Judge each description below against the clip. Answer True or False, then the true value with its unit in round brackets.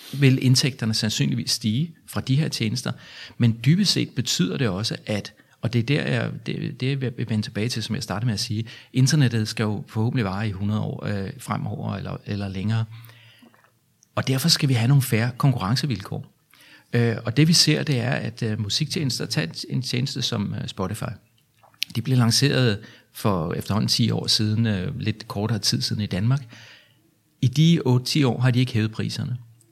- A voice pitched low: True (120 Hz)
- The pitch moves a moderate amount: True (3.5 semitones)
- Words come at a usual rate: True (180 wpm)